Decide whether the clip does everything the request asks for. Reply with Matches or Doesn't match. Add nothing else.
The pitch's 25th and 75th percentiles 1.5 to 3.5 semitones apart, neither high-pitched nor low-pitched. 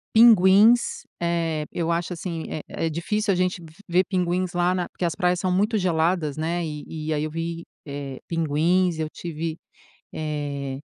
Matches